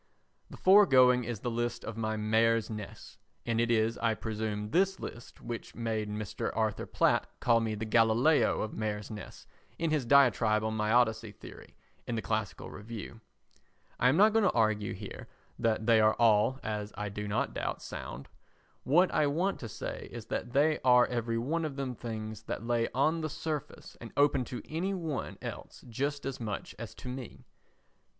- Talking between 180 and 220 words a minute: Yes, average, 185 wpm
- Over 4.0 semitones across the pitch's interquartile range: No, average, 3.7 semitones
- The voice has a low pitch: Yes, low, 115 Hz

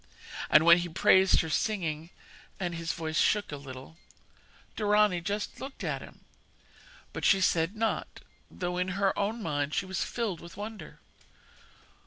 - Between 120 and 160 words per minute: Yes, average, 155 wpm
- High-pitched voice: No, medium, 180 Hz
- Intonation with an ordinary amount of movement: Yes, average, 4.0 semitones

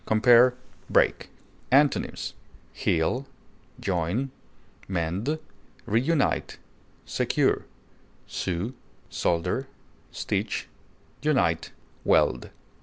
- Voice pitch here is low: Yes, low, 115 Hz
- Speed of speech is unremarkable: No, slow, 55 wpm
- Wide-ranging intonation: Yes, wide, 7.6 semitones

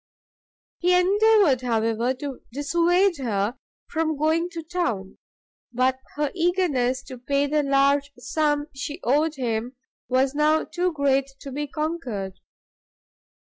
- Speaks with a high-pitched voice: Yes, very high, 285 Hz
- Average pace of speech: No, slow, 125 wpm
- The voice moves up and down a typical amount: Yes, average, 4.2 semitones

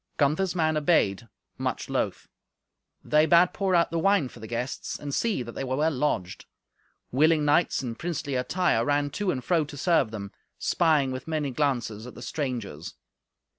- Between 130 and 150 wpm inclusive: No, average, 175 wpm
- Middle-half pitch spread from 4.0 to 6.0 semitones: Yes, average, 4.6 semitones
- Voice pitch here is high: No, medium, 145 Hz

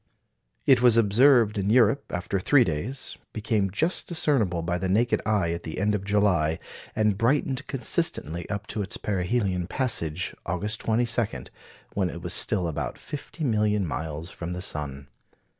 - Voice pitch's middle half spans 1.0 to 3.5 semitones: No, average, 5.2 semitones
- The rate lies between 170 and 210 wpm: No, average, 160 wpm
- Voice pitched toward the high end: No, low, 105 Hz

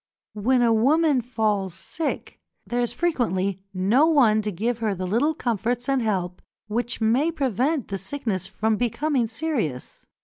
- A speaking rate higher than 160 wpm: No, average, 150 wpm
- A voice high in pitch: Yes, high, 230 Hz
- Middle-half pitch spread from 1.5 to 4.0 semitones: No, average, 4.4 semitones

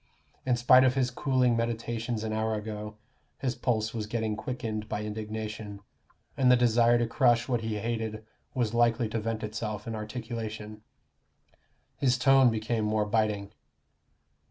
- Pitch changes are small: Yes, narrow, 1.9 semitones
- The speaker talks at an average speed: Yes, average, 150 wpm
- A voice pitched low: Yes, low, 110 Hz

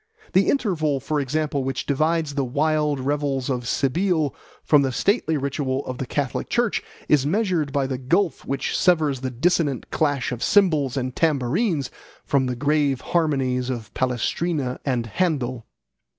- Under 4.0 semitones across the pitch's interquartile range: Yes, average, 3.4 semitones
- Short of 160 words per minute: Yes, average, 150 wpm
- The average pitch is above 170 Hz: No, medium, 140 Hz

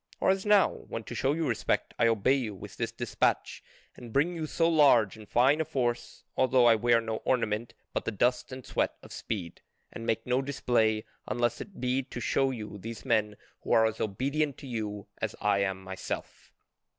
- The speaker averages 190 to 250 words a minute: Yes, average, 200 wpm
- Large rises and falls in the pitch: No, average, 3.6 semitones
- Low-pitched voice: Yes, low, 120 Hz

